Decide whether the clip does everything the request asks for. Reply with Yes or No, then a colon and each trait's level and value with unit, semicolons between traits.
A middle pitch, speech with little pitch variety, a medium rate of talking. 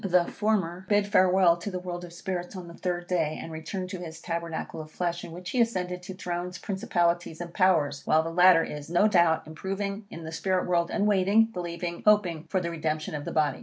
No: medium, 175 Hz; narrow, 2.2 semitones; fast, 220 wpm